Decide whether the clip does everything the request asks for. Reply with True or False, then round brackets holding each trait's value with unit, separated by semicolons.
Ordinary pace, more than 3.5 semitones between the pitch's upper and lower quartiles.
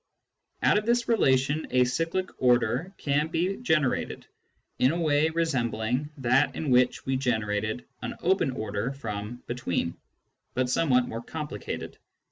True (145 wpm; 4.9 semitones)